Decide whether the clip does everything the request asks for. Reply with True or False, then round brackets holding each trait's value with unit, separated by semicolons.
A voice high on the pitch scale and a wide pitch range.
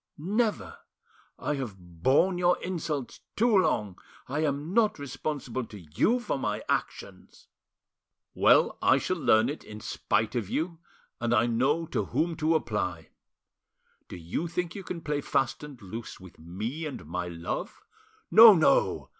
False (140 Hz; 8.0 semitones)